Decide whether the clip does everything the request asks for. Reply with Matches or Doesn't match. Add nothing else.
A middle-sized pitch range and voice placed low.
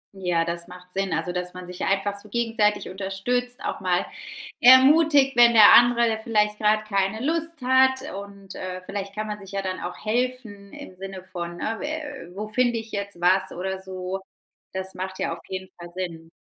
Doesn't match